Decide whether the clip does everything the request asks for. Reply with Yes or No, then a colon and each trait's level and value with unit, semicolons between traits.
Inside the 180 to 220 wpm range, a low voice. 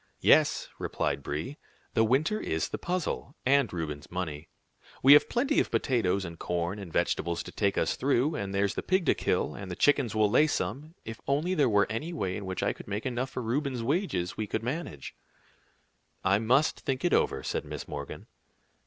Yes: average, 195 wpm; low, 115 Hz